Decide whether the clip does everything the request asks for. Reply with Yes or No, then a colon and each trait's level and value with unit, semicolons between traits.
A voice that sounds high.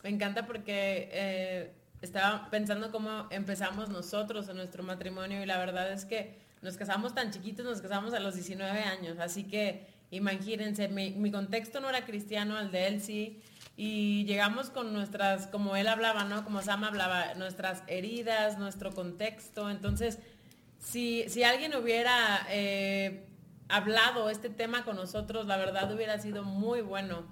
Yes: high, 205 Hz